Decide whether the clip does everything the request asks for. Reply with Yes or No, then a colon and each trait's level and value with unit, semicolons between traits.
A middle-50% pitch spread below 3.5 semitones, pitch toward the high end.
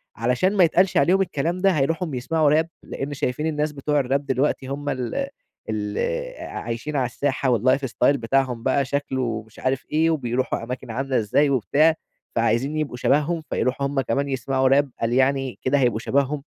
No: average, 3.1 semitones; low, 135 Hz